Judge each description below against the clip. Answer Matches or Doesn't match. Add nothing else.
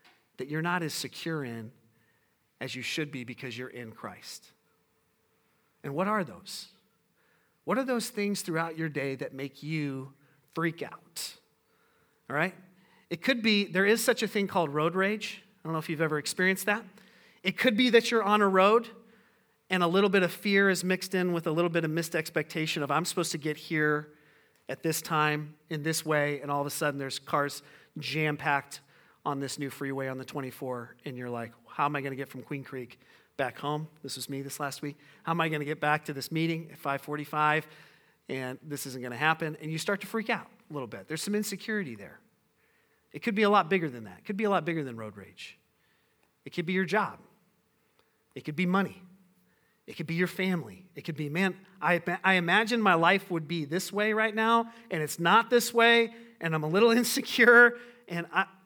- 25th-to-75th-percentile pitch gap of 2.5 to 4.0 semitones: Doesn't match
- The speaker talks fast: Matches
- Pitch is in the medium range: Matches